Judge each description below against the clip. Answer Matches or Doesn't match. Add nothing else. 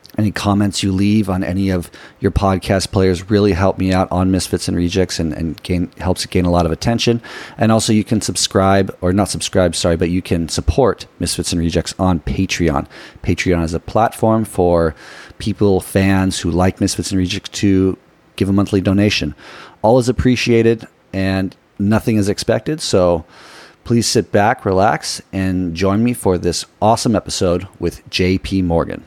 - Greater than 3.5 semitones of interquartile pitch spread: Doesn't match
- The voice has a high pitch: Doesn't match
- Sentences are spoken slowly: Doesn't match